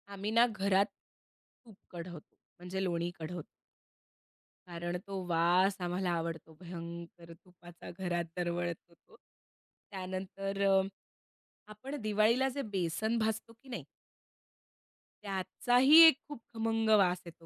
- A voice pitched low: No, medium, 185 Hz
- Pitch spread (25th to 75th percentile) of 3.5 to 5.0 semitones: Yes, average, 3.8 semitones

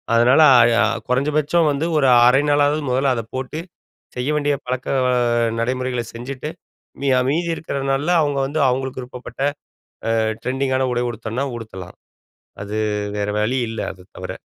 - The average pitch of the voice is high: No, low, 130 Hz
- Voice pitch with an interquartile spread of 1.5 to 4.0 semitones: Yes, average, 2.9 semitones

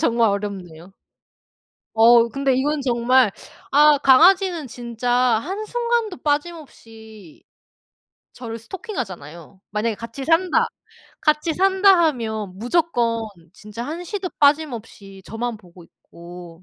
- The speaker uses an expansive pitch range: Yes, wide, 6.7 semitones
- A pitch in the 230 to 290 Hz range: Yes, high, 245 Hz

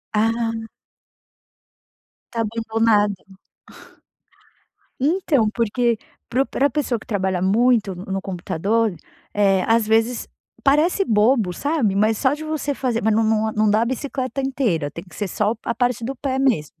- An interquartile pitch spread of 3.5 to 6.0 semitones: Yes, average, 4.0 semitones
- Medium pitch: No, high, 225 Hz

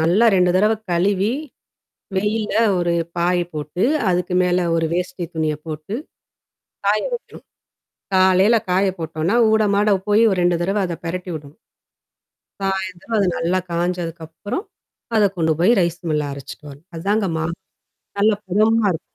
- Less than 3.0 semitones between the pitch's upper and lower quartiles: No, average, 3.4 semitones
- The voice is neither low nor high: Yes, medium, 180 Hz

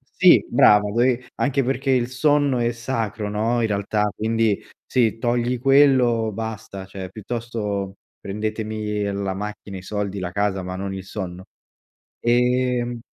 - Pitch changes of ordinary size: Yes, average, 3.2 semitones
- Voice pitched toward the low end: Yes, low, 110 Hz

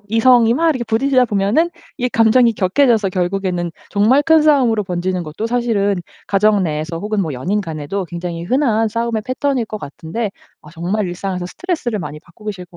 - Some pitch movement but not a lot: Yes, average, 5.0 semitones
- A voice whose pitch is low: No, high, 210 Hz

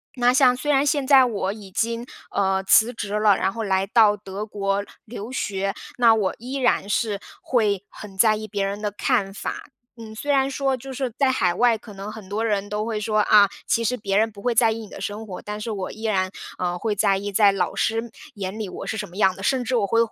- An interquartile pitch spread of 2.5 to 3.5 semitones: Yes, average, 2.9 semitones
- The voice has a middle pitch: No, high, 215 Hz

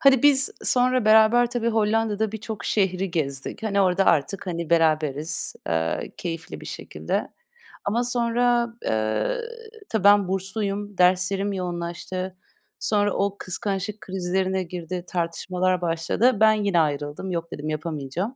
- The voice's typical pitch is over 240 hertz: No, high, 190 Hz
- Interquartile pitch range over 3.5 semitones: Yes, average, 4.2 semitones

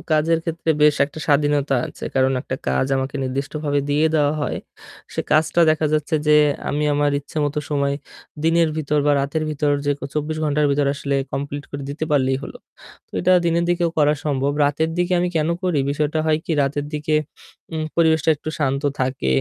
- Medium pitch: Yes, medium, 150 Hz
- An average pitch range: No, narrow, 1.8 semitones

